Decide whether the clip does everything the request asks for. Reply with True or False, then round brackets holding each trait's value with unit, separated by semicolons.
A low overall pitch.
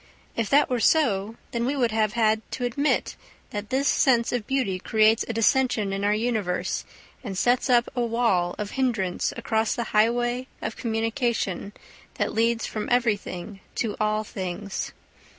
False (225 Hz)